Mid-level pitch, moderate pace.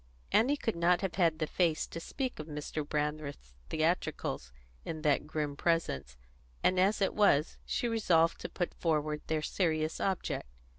Yes: medium, 160 Hz; average, 160 wpm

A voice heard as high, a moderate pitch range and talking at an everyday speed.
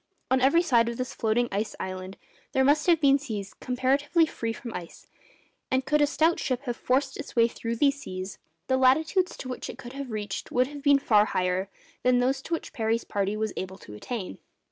No: very high, 250 Hz; average, 4.5 semitones; fast, 210 wpm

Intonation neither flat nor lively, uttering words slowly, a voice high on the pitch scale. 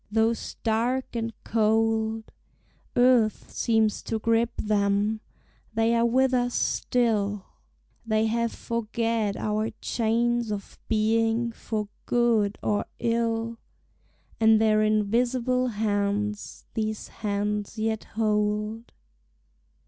No: narrow, 1.5 semitones; slow, 100 wpm; high, 225 Hz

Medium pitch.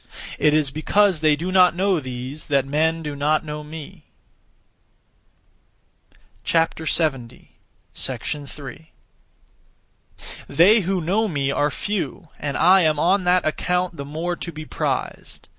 Yes: medium, 155 Hz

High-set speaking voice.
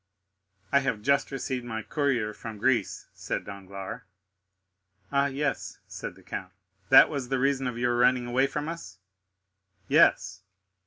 No: low, 130 Hz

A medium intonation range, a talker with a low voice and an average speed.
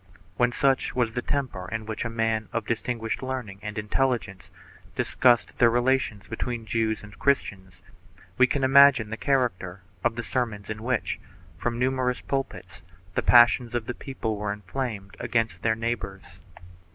Yes: average, 3.0 semitones; low, 115 Hz; average, 160 wpm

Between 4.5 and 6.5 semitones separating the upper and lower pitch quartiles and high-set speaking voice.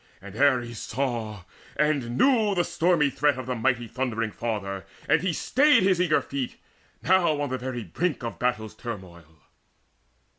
No: wide, 5.6 semitones; low, 130 Hz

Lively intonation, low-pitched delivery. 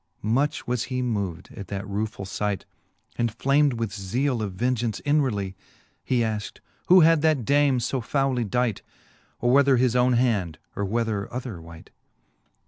No: average, 4.3 semitones; low, 120 Hz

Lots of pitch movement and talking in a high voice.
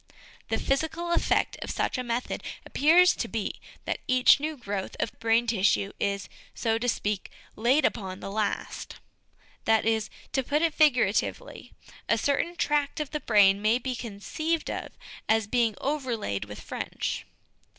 Yes: wide, 5.8 semitones; high, 240 Hz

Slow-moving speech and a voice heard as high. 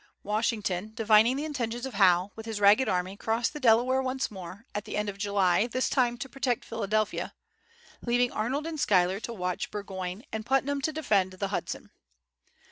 No: average, 180 wpm; high, 220 Hz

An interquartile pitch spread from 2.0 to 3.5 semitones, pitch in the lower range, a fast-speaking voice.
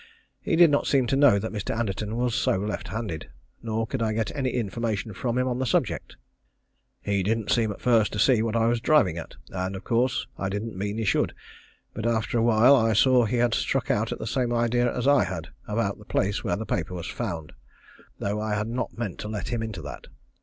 Yes: average, 2.9 semitones; low, 110 Hz; fast, 230 wpm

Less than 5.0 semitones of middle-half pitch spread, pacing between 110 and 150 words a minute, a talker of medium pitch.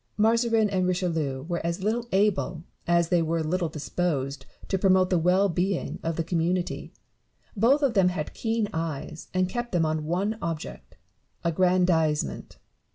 No: average, 3.1 semitones; average, 160 wpm; medium, 180 Hz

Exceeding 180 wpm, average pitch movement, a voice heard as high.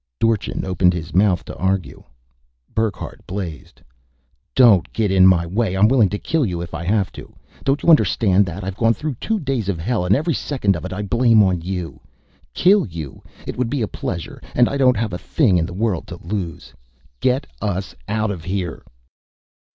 No: average, 195 wpm; average, 4.4 semitones; low, 100 Hz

